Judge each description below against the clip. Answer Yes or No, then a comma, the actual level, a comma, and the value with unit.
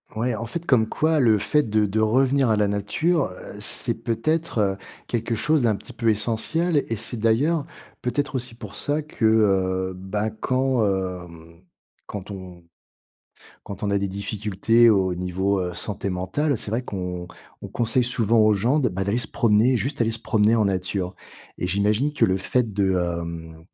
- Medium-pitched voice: No, low, 110 Hz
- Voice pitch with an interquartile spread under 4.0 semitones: No, average, 4.3 semitones